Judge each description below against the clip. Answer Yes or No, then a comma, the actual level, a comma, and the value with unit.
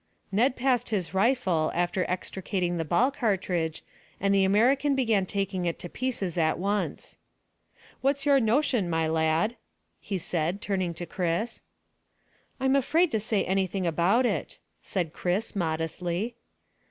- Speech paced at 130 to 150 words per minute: Yes, average, 140 wpm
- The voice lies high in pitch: Yes, high, 195 Hz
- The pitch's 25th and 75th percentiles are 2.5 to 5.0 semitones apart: No, wide, 5.4 semitones